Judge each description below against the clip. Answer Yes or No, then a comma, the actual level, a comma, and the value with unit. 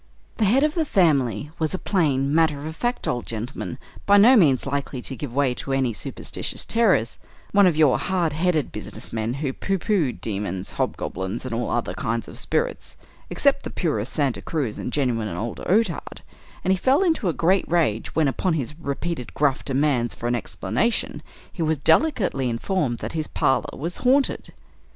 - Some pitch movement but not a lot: No, wide, 7.2 semitones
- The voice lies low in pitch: No, medium, 150 Hz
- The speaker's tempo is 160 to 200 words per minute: Yes, average, 185 wpm